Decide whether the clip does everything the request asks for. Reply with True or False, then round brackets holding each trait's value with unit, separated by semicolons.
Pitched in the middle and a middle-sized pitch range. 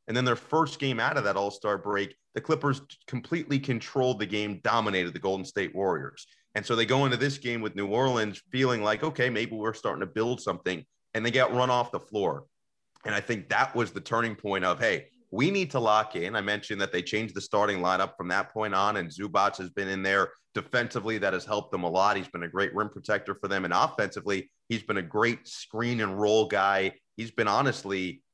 False (110 Hz; 3.8 semitones)